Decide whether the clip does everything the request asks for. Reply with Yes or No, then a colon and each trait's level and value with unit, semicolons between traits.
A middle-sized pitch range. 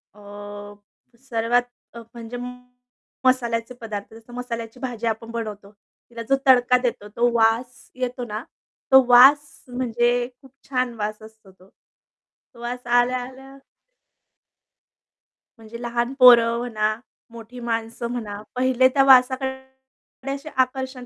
No: narrow, 2.0 semitones